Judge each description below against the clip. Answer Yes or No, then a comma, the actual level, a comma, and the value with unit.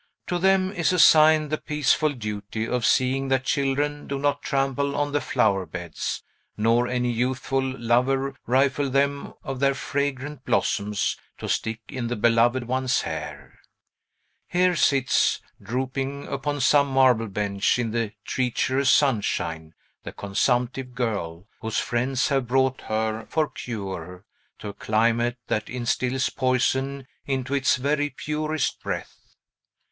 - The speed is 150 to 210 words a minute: No, slow, 135 wpm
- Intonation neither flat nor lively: Yes, average, 3.4 semitones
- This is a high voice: No, low, 130 Hz